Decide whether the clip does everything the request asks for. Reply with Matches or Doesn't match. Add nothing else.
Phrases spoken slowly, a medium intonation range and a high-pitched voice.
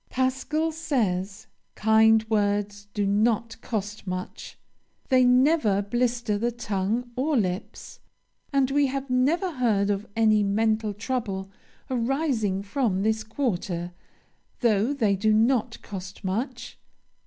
Matches